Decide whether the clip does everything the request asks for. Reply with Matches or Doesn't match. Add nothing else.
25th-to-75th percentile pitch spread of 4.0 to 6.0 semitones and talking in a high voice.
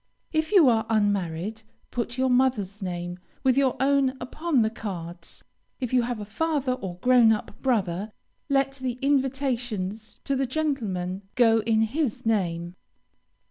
Matches